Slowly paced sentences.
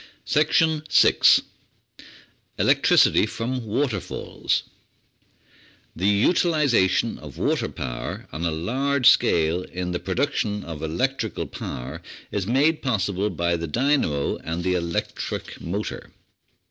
Yes: slow, 105 wpm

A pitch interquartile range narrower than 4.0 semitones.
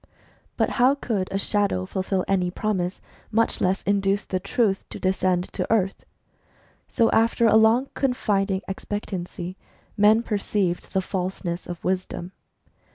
Yes: average, 2.7 semitones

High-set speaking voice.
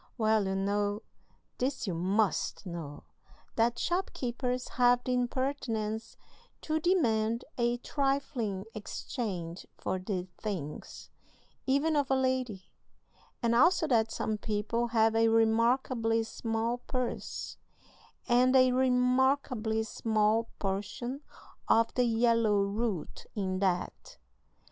Yes: high, 230 Hz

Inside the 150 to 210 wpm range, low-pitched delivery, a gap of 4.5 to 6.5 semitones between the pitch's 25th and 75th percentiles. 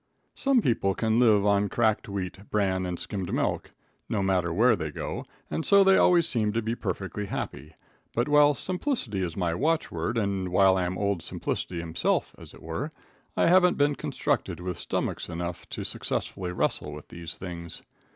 Yes: average, 180 wpm; low, 100 Hz; average, 5.1 semitones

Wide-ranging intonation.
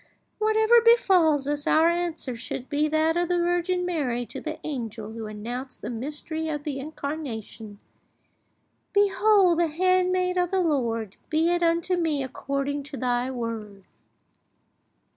Yes: wide, 5.8 semitones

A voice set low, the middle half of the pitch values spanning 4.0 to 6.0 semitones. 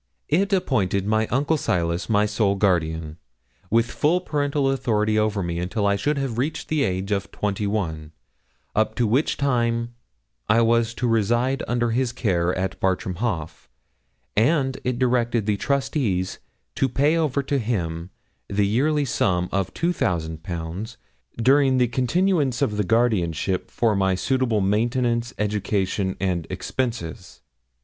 Yes: low, 110 Hz; average, 5.3 semitones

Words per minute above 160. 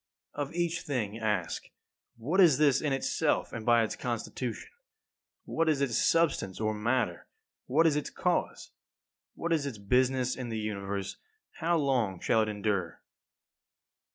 No: average, 155 wpm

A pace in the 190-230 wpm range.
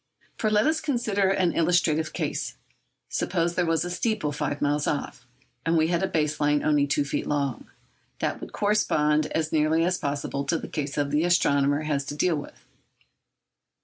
No: average, 180 wpm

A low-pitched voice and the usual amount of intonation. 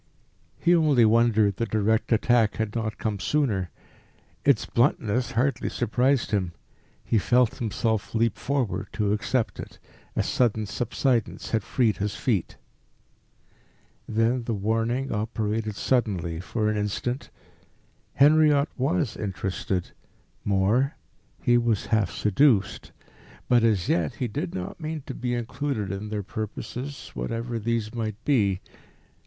Yes: low, 115 Hz; average, 3.1 semitones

